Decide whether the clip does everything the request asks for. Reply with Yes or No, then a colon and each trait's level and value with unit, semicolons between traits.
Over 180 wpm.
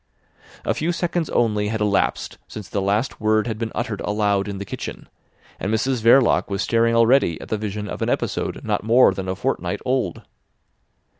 Yes: average, 190 wpm